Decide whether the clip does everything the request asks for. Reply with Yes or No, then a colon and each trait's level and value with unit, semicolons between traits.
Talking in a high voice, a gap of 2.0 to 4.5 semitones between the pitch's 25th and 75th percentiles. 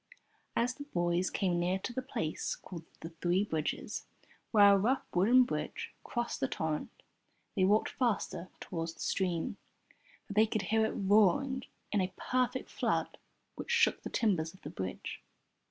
No: high, 195 Hz; average, 5.3 semitones